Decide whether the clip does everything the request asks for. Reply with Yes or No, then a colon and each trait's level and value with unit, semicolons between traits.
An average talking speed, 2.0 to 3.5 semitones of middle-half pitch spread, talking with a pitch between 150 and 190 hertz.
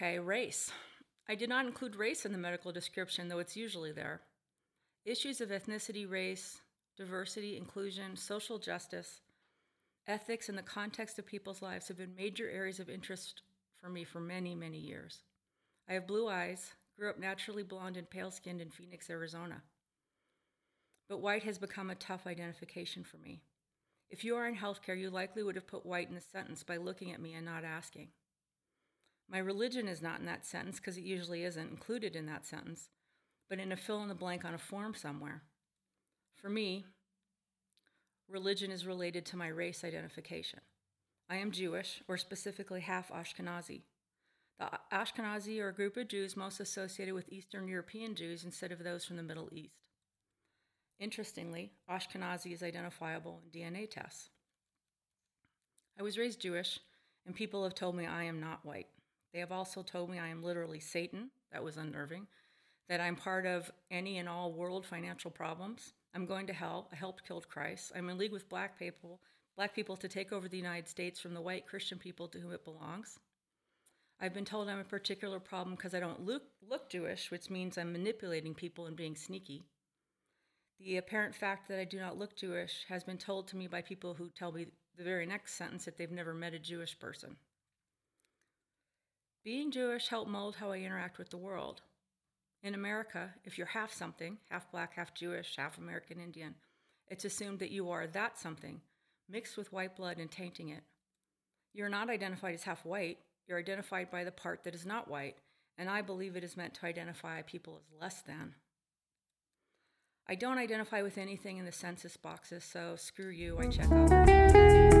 Yes: average, 185 wpm; narrow, 2.6 semitones; medium, 185 Hz